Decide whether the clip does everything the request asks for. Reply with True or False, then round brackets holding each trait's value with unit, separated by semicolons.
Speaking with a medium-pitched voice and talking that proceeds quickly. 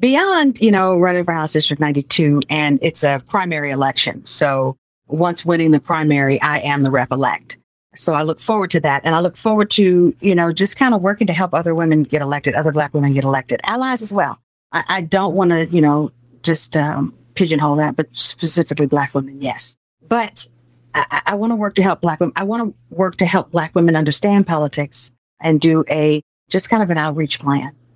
True (155 Hz; 210 wpm)